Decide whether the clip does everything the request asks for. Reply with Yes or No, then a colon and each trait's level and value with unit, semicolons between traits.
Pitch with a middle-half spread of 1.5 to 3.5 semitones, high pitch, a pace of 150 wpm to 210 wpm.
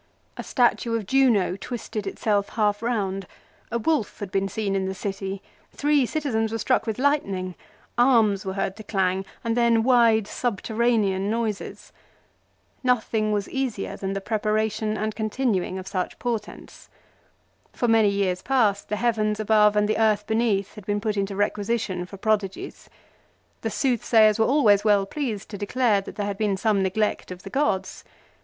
Yes: average, 2.7 semitones; high, 215 Hz; average, 165 wpm